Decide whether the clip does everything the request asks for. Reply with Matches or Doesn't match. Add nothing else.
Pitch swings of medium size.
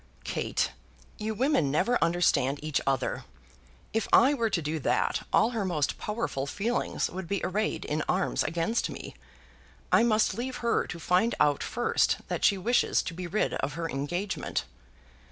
Doesn't match